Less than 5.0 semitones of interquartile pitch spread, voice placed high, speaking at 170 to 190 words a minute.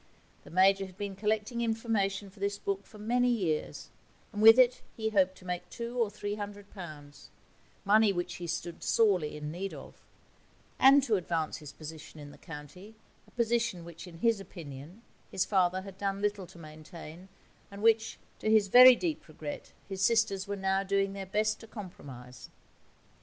Yes: average, 3.9 semitones; high, 195 Hz; average, 180 wpm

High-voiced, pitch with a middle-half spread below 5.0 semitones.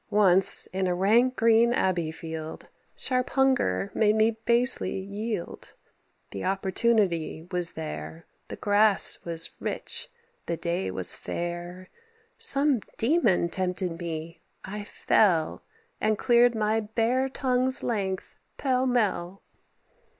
No: high, 200 Hz; average, 5.3 semitones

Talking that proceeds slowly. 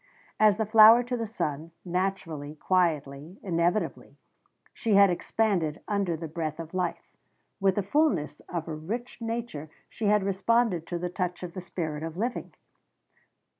No: average, 155 wpm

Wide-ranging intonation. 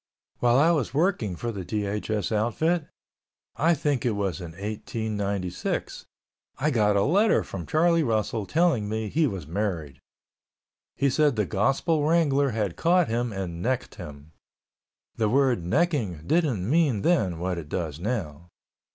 Yes: wide, 7.3 semitones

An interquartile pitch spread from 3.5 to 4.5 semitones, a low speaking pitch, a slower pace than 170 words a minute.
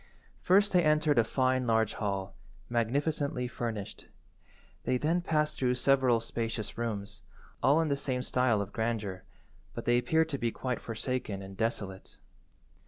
Yes: average, 4.1 semitones; low, 120 Hz; average, 150 wpm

